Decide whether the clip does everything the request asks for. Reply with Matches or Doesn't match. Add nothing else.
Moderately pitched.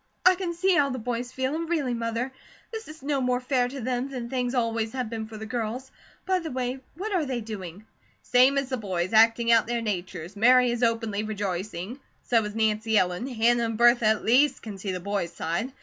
Doesn't match